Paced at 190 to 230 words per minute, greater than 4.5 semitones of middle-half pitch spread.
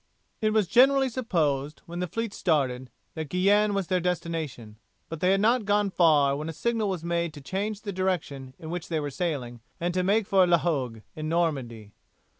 Yes: average, 200 wpm; average, 5.2 semitones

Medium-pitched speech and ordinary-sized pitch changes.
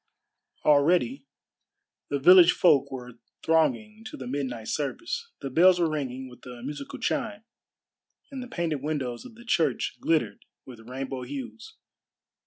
No: medium, 150 Hz; wide, 6.2 semitones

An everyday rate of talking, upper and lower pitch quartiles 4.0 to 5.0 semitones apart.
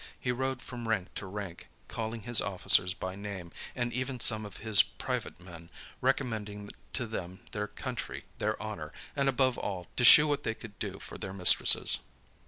Yes: average, 180 wpm; average, 4.3 semitones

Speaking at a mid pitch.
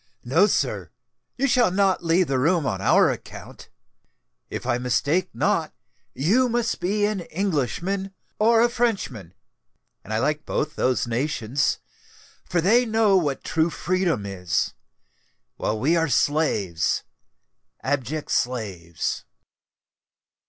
Yes: medium, 160 Hz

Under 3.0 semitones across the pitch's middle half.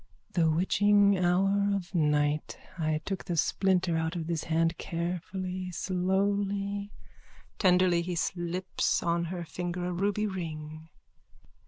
Yes: narrow, 2.5 semitones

